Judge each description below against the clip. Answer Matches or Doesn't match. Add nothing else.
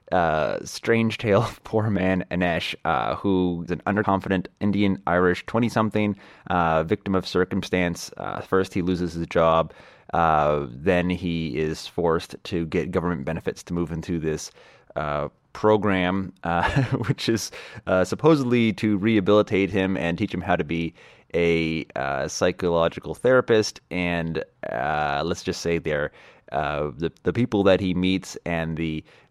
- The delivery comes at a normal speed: Matches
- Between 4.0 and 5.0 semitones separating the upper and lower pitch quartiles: Doesn't match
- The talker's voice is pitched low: Matches